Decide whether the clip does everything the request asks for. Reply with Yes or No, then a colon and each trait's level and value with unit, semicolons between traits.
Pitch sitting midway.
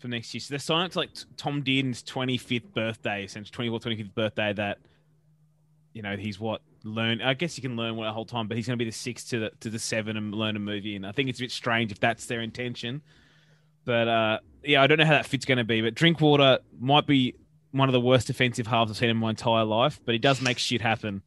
No: low, 120 Hz